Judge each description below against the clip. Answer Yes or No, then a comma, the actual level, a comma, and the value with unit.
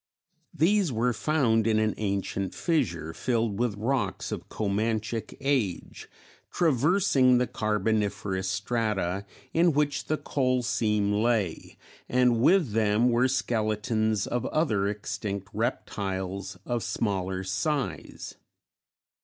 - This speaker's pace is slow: Yes, slow, 110 wpm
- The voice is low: Yes, low, 110 Hz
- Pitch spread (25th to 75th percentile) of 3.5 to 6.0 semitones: Yes, average, 4.0 semitones